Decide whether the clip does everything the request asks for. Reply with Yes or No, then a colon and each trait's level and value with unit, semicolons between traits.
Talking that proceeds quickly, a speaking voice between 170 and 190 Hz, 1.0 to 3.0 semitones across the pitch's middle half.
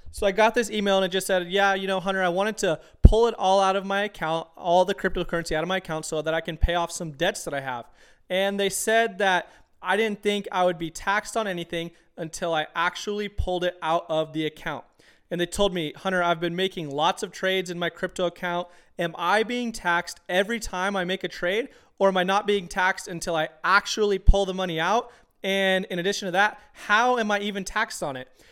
Yes: fast, 240 wpm; medium, 185 Hz; average, 2.7 semitones